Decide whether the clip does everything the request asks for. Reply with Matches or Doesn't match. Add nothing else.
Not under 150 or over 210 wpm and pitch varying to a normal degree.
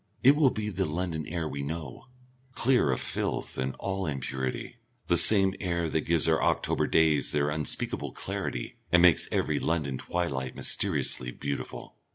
Matches